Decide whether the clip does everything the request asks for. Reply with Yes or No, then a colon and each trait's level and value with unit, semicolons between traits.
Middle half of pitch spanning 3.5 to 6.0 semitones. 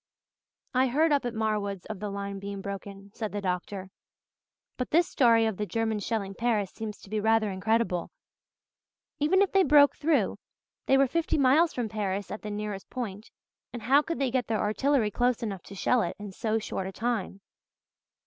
Yes: average, 4.0 semitones